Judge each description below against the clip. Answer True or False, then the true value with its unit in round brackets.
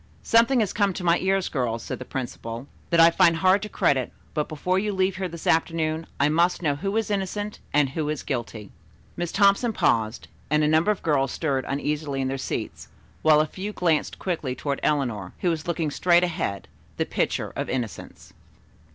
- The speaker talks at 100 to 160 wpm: False (195 wpm)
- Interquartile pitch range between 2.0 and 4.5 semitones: False (5.1 semitones)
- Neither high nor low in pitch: True (160 Hz)